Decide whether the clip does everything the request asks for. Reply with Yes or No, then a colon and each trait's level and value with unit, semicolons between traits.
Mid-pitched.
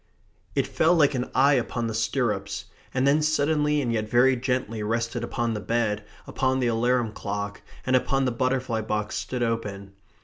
No: low, 120 Hz